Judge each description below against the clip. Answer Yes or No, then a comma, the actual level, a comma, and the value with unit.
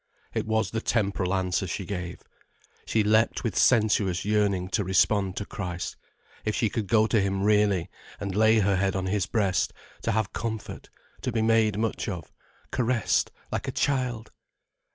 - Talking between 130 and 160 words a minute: No, average, 170 wpm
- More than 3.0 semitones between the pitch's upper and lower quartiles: No, narrow, 2.6 semitones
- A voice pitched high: No, low, 105 Hz